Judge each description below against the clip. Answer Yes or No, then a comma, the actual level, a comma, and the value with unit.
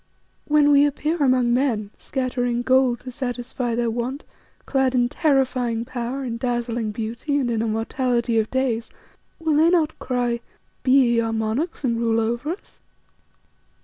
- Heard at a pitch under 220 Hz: No, high, 245 Hz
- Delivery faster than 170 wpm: No, average, 150 wpm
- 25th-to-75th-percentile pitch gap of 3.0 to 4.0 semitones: No, narrow, 2.5 semitones